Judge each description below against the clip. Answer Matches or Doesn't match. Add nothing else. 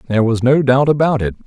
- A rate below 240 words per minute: Doesn't match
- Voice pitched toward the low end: Matches